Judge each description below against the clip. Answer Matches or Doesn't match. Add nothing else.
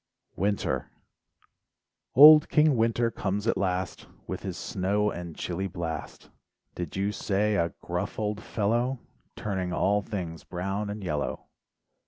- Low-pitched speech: Matches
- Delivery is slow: Matches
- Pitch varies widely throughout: Doesn't match